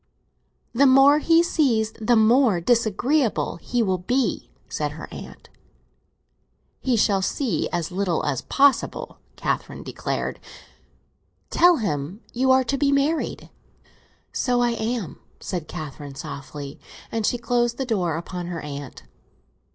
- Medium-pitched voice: No, high, 225 Hz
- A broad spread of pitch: Yes, wide, 7.0 semitones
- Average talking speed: No, slow, 130 wpm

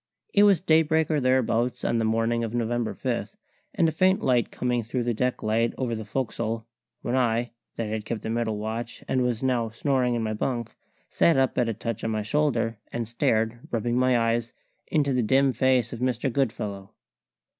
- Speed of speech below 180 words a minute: No, average, 195 wpm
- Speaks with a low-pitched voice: Yes, low, 120 Hz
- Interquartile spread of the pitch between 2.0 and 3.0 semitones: Yes, narrow, 2.4 semitones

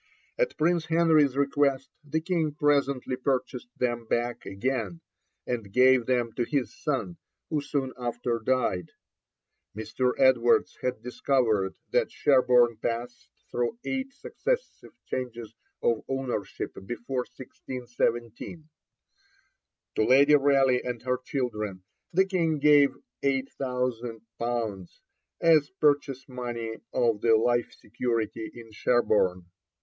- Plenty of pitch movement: No, average, 3.2 semitones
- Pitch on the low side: Yes, low, 125 Hz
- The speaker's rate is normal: No, slow, 110 wpm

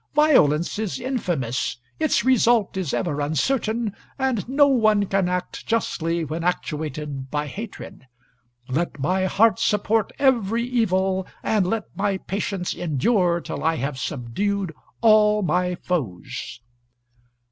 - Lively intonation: Yes, wide, 5.9 semitones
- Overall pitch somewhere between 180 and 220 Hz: Yes, high, 190 Hz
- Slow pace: Yes, slow, 125 wpm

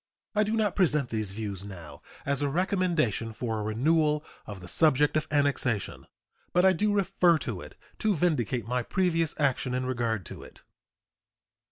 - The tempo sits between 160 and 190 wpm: Yes, average, 170 wpm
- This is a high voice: No, medium, 145 Hz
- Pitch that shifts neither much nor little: No, wide, 7.4 semitones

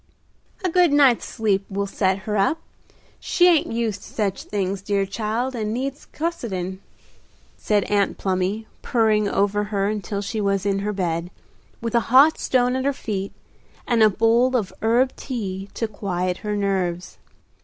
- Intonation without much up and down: No, average, 3.4 semitones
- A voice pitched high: Yes, high, 210 Hz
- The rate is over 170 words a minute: No, average, 165 wpm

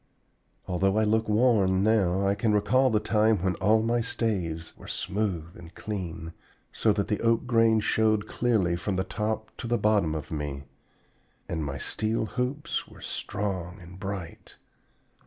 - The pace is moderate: Yes, average, 160 wpm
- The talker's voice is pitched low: Yes, low, 105 Hz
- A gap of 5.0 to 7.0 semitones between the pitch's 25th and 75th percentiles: No, average, 3.7 semitones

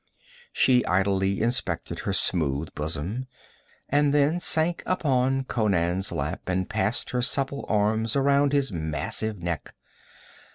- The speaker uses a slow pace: Yes, slow, 120 wpm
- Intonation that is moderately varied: No, wide, 7.3 semitones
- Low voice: Yes, low, 110 Hz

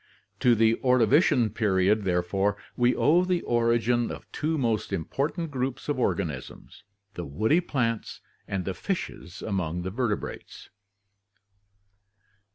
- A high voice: No, low, 115 Hz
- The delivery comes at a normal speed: No, slow, 120 wpm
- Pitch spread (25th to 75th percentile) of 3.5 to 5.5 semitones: Yes, average, 5.1 semitones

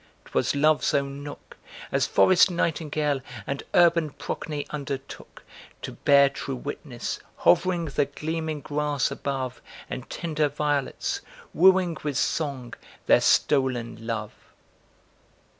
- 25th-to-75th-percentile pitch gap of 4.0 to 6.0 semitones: No, narrow, 2.4 semitones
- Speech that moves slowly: Yes, slow, 110 wpm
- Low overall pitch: No, medium, 145 Hz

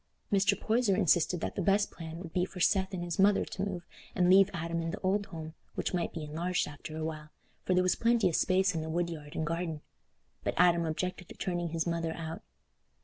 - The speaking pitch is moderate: Yes, medium, 175 Hz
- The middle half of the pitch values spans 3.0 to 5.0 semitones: No, narrow, 2.6 semitones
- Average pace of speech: No, fast, 225 wpm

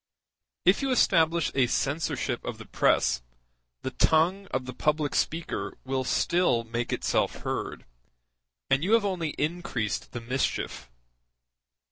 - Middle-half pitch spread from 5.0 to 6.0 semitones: Yes, wide, 5.4 semitones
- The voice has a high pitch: No, medium, 155 Hz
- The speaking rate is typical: No, slow, 130 wpm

